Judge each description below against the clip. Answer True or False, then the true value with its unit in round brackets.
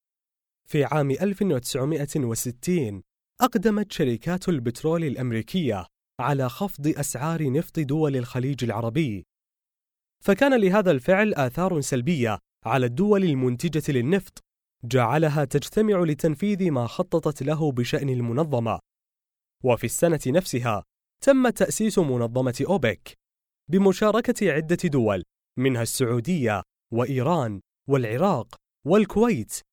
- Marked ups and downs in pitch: True (6.5 semitones)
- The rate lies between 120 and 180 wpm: False (95 wpm)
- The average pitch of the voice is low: False (150 Hz)